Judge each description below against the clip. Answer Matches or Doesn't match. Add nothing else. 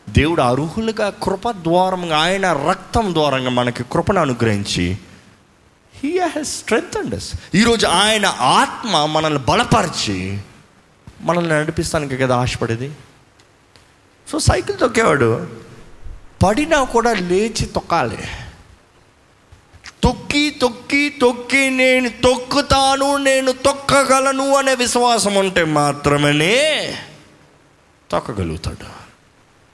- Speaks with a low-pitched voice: Doesn't match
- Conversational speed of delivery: Matches